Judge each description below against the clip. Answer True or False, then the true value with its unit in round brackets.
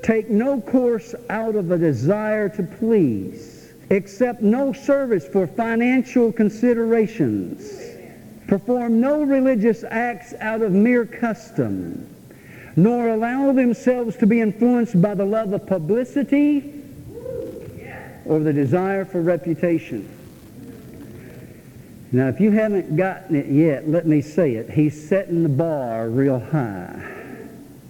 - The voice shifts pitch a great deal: True (6.3 semitones)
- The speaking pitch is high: True (210 Hz)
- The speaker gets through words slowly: True (120 wpm)